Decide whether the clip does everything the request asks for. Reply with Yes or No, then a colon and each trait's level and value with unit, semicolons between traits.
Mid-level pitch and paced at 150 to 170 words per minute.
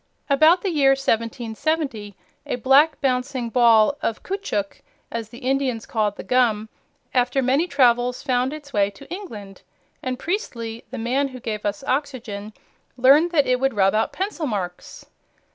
No: very high, 250 Hz; average, 155 wpm